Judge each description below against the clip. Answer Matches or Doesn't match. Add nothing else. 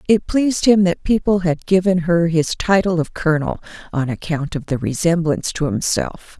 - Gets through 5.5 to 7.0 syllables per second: Doesn't match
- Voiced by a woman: Matches